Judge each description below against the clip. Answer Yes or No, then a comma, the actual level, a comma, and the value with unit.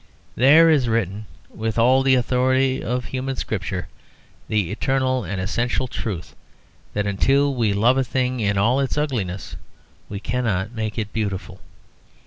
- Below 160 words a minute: Yes, average, 150 wpm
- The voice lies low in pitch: Yes, low, 115 Hz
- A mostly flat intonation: No, average, 4.3 semitones